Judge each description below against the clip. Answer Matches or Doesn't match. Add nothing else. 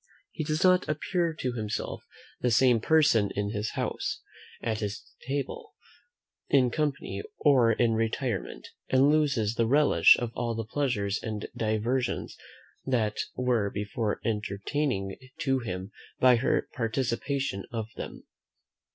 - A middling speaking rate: Doesn't match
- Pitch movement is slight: Doesn't match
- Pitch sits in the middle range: Doesn't match